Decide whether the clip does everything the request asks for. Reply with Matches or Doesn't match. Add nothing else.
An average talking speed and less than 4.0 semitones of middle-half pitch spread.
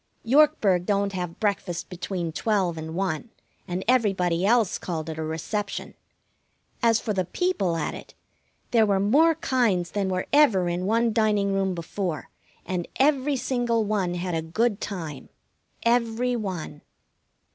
Doesn't match